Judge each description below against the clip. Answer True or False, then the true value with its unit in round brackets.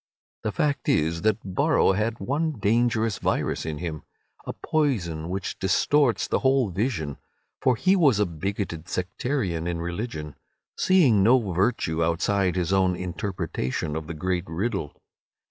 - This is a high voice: False (95 Hz)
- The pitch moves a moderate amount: False (5.7 semitones)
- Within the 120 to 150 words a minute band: True (135 wpm)